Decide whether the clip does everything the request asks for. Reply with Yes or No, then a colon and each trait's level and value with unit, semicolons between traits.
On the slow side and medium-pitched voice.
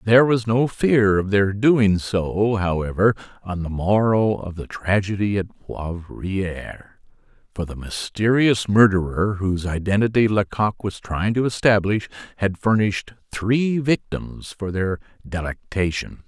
No: slow, 130 wpm; low, 100 Hz